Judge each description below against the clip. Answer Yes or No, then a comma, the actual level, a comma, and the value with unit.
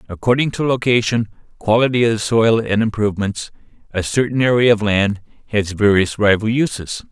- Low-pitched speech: Yes, low, 110 Hz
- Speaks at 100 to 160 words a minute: Yes, average, 150 wpm